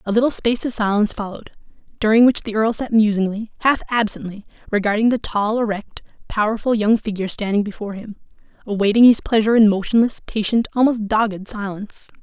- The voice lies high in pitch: Yes, high, 215 Hz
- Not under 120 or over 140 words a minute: No, average, 160 wpm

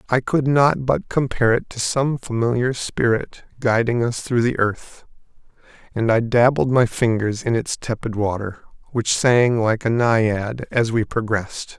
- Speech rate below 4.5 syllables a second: Yes, 4.3 syllables/s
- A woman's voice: No, male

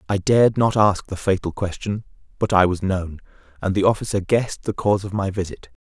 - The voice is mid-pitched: No, very low, 95 Hz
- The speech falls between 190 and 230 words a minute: Yes, fast, 205 wpm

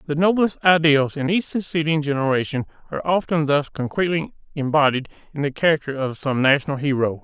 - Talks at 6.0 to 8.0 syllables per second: Yes, 6.1 syllables/s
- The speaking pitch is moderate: Yes, medium, 150 Hz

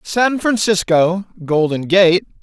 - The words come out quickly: No, slow, 100 wpm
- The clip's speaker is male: Yes, male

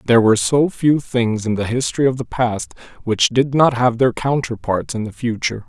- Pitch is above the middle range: No, low, 120 Hz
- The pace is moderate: No, fast, 220 wpm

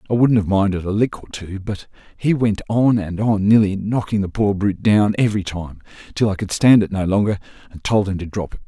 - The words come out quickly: Yes, fast, 240 wpm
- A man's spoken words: Yes, male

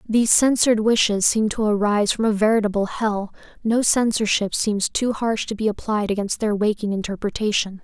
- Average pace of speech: Yes, average, 170 wpm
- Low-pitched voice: No, high, 210 Hz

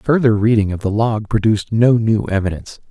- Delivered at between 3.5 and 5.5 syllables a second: No, 5.7 syllables/s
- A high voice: No, low, 110 Hz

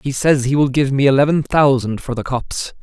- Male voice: Yes, male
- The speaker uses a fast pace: Yes, fast, 235 wpm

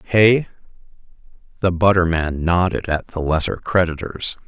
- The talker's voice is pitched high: No, very low, 90 Hz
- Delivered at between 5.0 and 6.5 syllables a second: No, 4.4 syllables/s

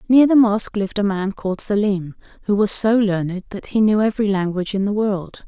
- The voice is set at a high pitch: Yes, high, 205 Hz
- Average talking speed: No, fast, 220 wpm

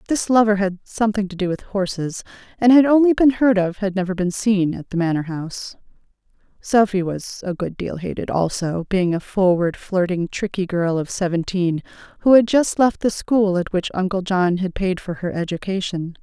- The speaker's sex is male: No, female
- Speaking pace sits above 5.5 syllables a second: No, 5.1 syllables/s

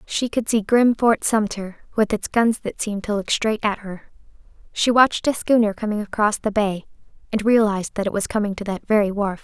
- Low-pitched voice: No, high, 210 Hz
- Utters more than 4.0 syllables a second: Yes, 5.5 syllables/s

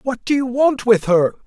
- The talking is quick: Yes, fast, 245 wpm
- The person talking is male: Yes, male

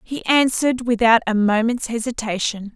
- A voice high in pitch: Yes, high, 230 Hz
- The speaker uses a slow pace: Yes, slow, 130 wpm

